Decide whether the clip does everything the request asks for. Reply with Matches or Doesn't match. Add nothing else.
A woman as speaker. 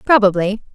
Matches